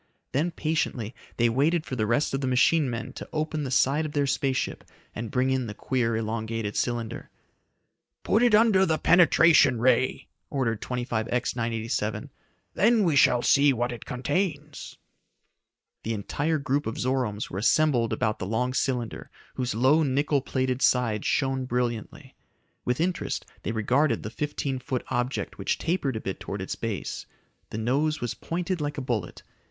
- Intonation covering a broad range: No, average, 4.3 semitones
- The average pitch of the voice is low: Yes, low, 130 Hz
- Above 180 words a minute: No, average, 165 wpm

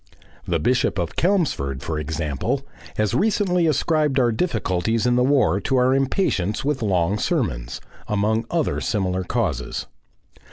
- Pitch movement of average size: No, wide, 7.6 semitones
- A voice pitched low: Yes, low, 110 Hz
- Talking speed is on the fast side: No, slow, 135 wpm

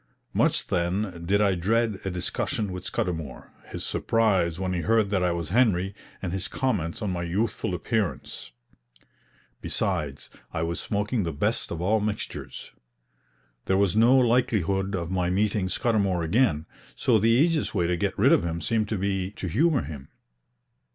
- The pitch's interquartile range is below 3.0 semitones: No, average, 4.1 semitones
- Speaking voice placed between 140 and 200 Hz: No, very low, 95 Hz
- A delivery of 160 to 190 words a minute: Yes, average, 165 wpm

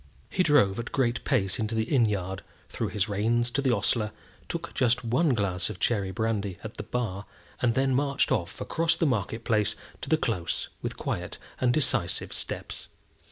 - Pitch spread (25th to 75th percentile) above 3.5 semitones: Yes, average, 4.2 semitones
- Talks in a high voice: No, low, 115 Hz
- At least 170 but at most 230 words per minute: Yes, average, 190 wpm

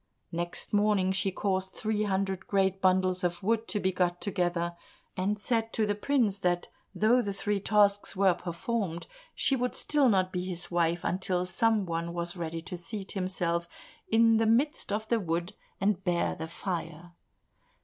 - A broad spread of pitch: No, average, 3.2 semitones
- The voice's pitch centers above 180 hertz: Yes, high, 190 Hz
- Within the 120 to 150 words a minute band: No, average, 170 wpm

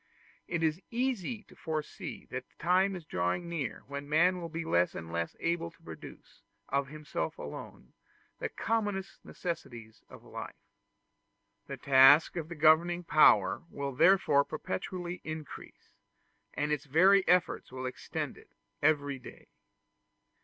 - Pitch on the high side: No, medium, 155 Hz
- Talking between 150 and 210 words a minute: No, average, 140 wpm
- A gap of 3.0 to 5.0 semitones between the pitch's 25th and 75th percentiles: Yes, average, 4.1 semitones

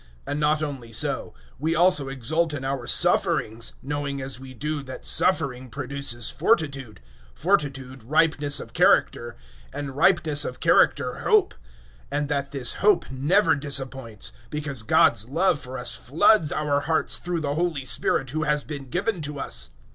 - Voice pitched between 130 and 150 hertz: Yes, medium, 140 Hz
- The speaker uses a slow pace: No, average, 160 wpm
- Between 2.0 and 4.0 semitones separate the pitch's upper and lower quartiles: Yes, average, 2.7 semitones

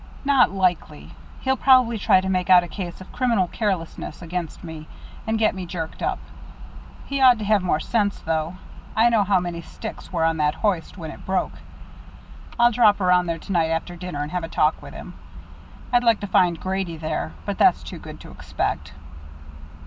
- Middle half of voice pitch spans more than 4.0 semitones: Yes, average, 4.5 semitones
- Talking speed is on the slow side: No, average, 195 wpm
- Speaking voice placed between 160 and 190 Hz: Yes, medium, 185 Hz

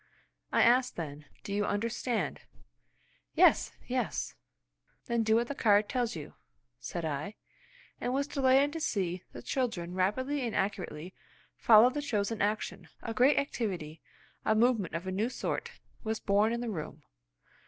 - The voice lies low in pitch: No, high, 220 Hz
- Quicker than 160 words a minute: No, average, 155 wpm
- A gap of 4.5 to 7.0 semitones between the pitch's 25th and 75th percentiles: Yes, average, 4.9 semitones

